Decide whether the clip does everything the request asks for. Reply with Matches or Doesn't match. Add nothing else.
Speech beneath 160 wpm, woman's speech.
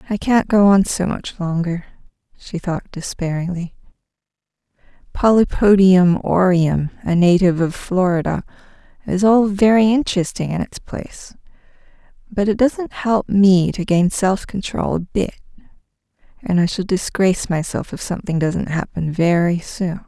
Matches